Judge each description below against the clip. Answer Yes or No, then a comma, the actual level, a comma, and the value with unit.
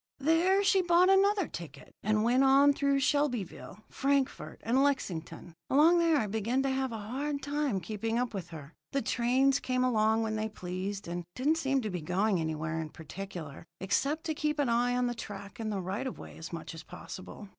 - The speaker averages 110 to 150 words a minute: No, average, 195 wpm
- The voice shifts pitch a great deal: Yes, wide, 6.5 semitones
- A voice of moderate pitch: No, high, 235 Hz